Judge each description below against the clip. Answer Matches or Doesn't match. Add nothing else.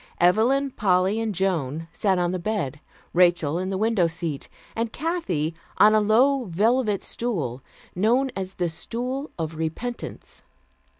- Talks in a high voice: Matches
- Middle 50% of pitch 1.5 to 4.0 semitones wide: Doesn't match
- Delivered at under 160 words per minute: Matches